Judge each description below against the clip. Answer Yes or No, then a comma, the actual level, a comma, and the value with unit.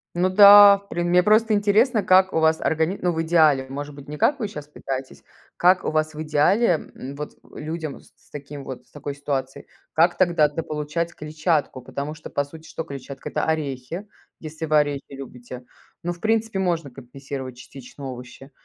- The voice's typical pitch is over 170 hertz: No, medium, 155 Hz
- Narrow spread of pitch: No, average, 3.9 semitones